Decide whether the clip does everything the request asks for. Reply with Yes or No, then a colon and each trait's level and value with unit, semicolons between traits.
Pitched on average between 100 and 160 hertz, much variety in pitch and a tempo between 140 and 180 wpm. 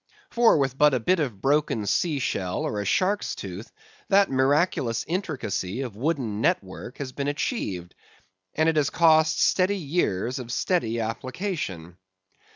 Yes: low, 135 Hz; wide, 6.5 semitones; average, 155 wpm